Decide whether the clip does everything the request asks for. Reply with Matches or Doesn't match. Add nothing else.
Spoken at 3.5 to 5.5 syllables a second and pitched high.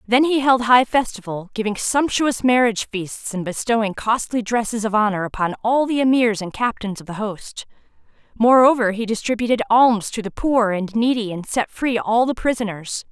Matches